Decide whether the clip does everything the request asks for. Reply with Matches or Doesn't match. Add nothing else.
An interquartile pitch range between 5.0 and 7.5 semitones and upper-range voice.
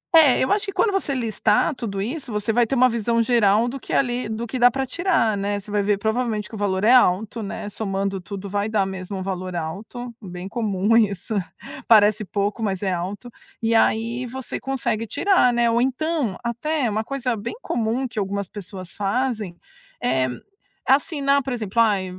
Doesn't match